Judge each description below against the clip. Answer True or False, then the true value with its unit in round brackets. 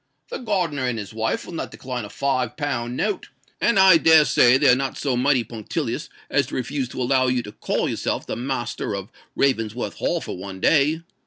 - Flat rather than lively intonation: False (3.6 semitones)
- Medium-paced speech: False (210 wpm)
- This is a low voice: True (130 Hz)